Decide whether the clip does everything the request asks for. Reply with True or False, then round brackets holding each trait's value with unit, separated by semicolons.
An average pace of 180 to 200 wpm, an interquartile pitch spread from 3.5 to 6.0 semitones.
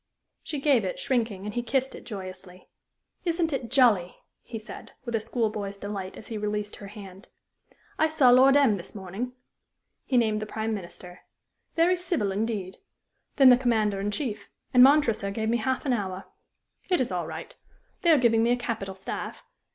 True (185 wpm; 4.4 semitones)